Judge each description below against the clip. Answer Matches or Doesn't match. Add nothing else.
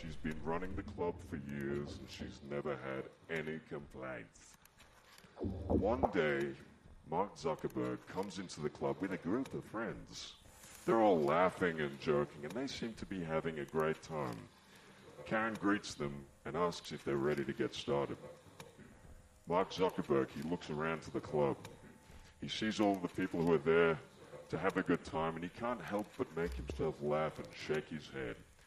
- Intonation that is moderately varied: Matches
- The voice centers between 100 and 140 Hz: Doesn't match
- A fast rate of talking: Doesn't match